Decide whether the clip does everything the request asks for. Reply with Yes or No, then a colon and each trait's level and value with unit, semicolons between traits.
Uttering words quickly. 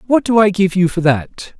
Yes: fast, 265 wpm